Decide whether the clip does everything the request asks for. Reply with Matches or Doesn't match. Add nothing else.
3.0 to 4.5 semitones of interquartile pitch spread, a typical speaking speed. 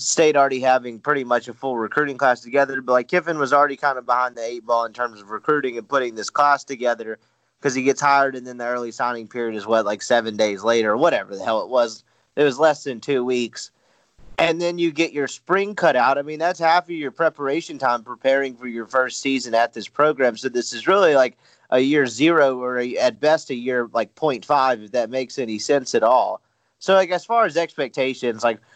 Doesn't match